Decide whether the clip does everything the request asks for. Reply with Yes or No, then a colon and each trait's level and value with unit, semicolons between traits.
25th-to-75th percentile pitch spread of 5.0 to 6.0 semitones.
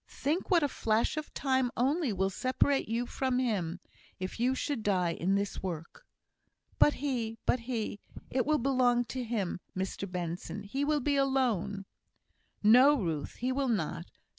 Yes: wide, 5.4 semitones